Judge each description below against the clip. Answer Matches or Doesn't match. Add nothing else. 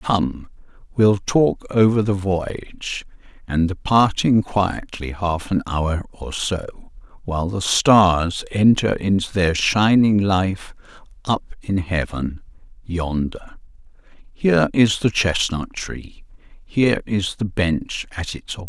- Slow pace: Matches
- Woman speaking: Doesn't match